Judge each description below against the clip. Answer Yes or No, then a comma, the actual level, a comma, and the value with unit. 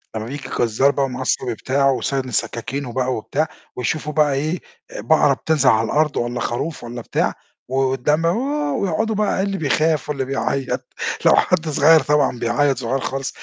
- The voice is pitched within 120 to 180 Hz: Yes, medium, 140 Hz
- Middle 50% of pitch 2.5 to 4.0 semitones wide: Yes, average, 3.4 semitones